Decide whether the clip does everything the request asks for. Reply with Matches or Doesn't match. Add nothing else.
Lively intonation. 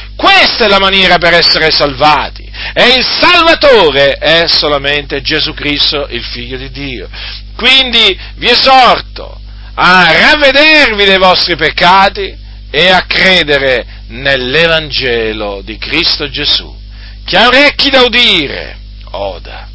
Matches